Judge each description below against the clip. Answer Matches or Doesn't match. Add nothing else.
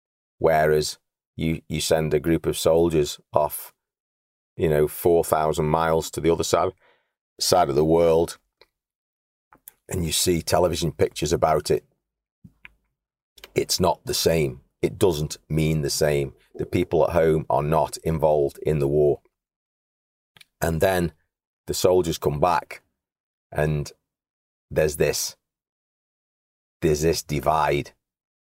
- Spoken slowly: Matches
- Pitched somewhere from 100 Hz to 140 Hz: Doesn't match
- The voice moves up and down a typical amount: Doesn't match